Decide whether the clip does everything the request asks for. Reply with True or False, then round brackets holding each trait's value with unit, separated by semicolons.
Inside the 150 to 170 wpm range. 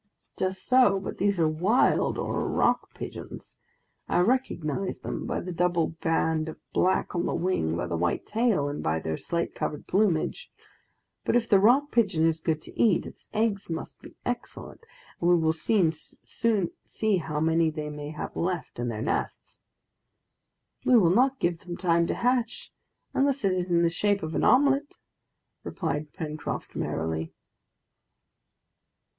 True (160 wpm)